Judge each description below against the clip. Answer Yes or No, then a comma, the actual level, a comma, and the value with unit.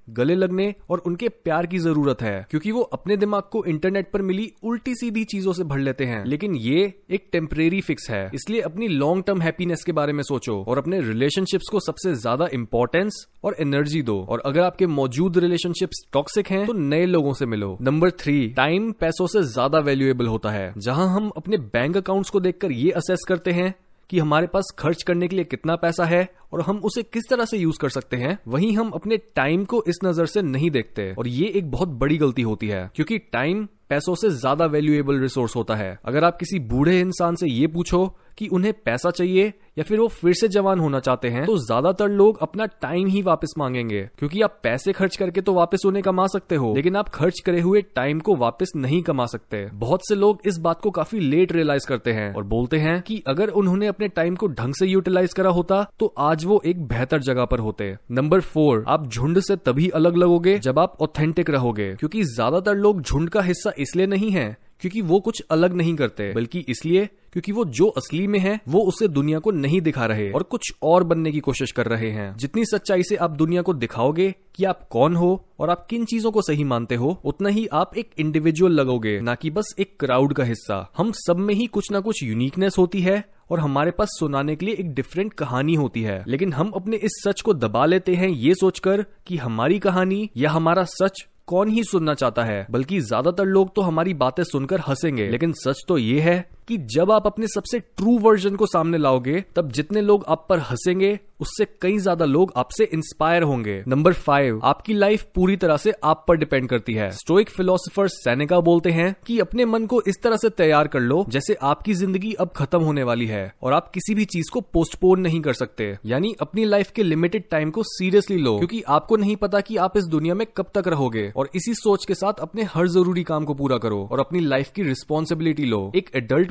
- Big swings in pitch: Yes, wide, 5.8 semitones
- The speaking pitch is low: No, medium, 175 Hz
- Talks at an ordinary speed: No, fast, 220 wpm